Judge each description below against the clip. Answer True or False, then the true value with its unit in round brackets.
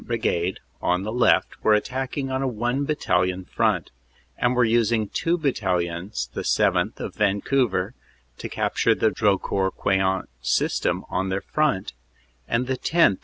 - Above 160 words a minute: False (145 wpm)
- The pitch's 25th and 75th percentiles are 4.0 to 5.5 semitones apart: True (5.2 semitones)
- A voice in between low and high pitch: False (105 Hz)